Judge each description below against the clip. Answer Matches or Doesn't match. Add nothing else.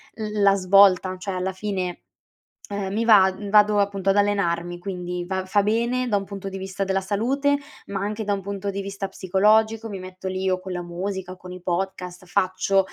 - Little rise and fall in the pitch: Matches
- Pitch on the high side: Matches